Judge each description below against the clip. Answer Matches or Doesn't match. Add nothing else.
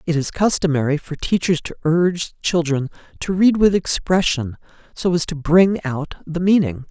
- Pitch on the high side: Doesn't match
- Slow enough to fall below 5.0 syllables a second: Matches